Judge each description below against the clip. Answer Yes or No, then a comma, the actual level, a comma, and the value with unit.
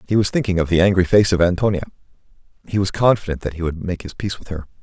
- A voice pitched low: Yes, very low, 95 Hz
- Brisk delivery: Yes, fast, 250 wpm